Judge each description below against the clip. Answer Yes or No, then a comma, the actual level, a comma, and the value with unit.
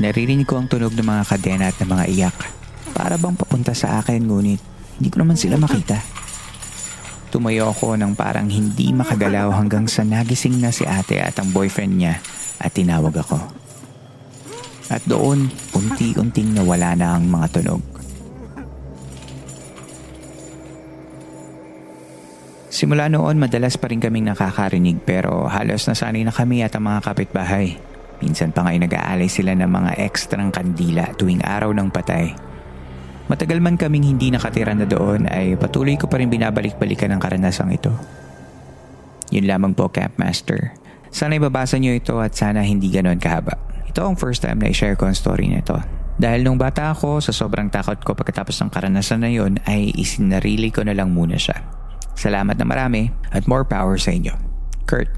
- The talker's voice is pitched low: Yes, low, 105 Hz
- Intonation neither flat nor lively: No, wide, 5.7 semitones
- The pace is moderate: No, fast, 165 wpm